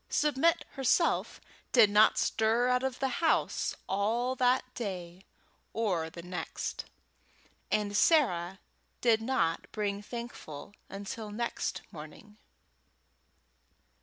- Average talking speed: No, slow, 105 wpm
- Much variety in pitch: No, average, 4.4 semitones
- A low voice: No, high, 220 Hz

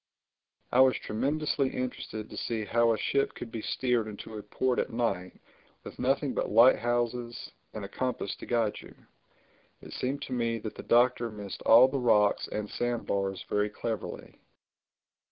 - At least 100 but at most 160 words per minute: No, average, 170 wpm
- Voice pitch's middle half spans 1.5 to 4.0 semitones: Yes, average, 2.9 semitones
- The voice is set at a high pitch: No, low, 120 Hz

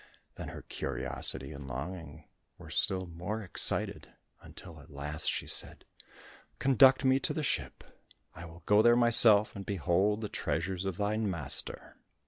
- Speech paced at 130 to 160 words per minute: Yes, average, 150 wpm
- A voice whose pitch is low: Yes, very low, 95 Hz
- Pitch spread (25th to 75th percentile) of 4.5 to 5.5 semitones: Yes, average, 4.9 semitones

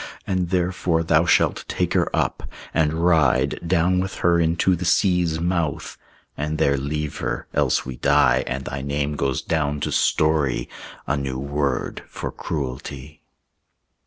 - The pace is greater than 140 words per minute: Yes, average, 150 wpm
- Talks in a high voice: No, very low, 75 Hz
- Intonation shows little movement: No, average, 3.4 semitones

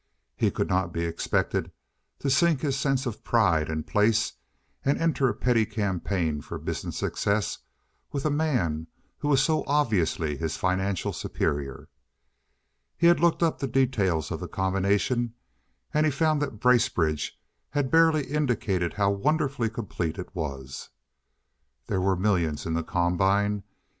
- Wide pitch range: Yes, wide, 7.9 semitones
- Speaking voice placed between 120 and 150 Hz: No, low, 105 Hz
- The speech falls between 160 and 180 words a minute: No, average, 150 wpm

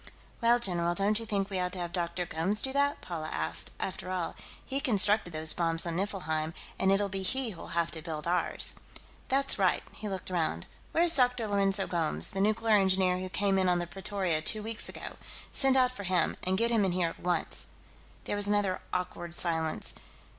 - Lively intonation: No, average, 3.5 semitones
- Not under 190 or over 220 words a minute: Yes, fast, 205 wpm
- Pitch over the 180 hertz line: Yes, high, 190 Hz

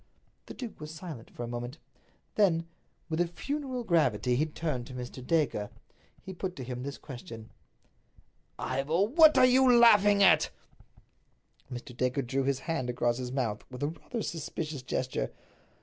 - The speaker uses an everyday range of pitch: No, wide, 7.0 semitones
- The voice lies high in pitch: No, medium, 150 Hz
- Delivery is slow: No, average, 155 wpm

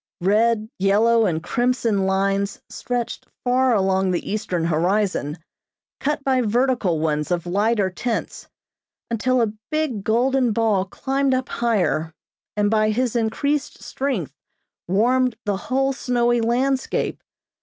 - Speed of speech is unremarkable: No, slow, 125 wpm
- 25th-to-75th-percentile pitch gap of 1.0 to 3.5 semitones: No, average, 4.7 semitones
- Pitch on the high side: Yes, high, 225 Hz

